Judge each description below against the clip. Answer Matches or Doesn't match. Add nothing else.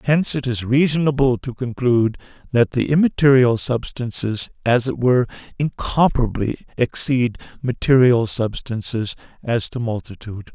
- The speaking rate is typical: Doesn't match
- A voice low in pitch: Matches